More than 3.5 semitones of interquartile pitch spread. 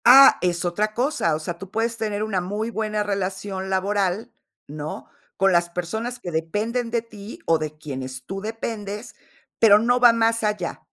Yes: average, 4.2 semitones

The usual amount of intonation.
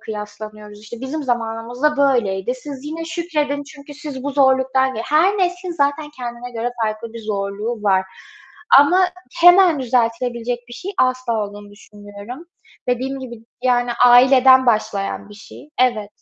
Yes: average, 4.5 semitones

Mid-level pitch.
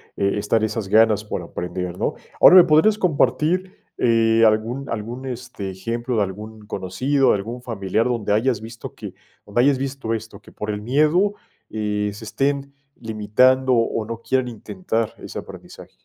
No: low, 115 Hz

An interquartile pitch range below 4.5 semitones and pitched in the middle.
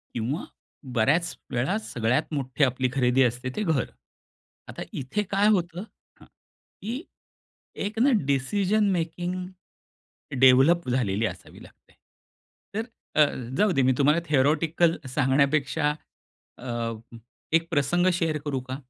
No: average, 5.1 semitones; medium, 150 Hz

